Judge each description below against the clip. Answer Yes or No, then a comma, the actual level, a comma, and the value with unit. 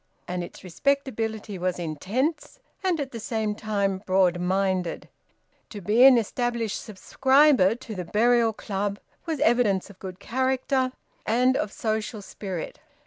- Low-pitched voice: No, high, 215 Hz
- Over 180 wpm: No, average, 140 wpm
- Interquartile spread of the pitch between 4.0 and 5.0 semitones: Yes, average, 4.7 semitones